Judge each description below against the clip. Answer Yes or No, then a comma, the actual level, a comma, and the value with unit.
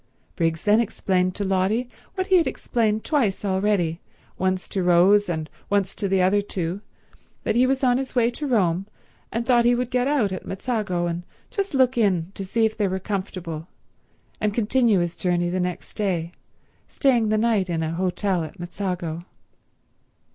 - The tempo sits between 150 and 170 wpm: No, average, 180 wpm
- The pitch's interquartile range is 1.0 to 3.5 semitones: No, average, 4.6 semitones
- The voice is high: Yes, high, 195 Hz